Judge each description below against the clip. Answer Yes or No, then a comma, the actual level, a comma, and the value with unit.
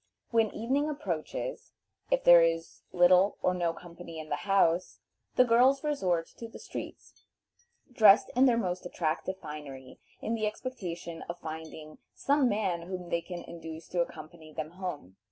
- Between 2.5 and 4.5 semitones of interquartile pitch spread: No, average, 4.9 semitones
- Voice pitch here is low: No, medium, 175 Hz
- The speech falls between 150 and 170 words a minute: Yes, average, 155 wpm